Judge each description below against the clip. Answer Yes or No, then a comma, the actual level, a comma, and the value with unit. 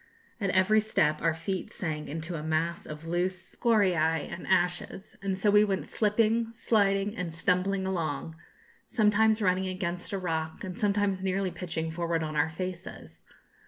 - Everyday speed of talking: Yes, average, 160 wpm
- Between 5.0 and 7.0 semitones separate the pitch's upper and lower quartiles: No, average, 3.4 semitones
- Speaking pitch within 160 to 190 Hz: Yes, medium, 185 Hz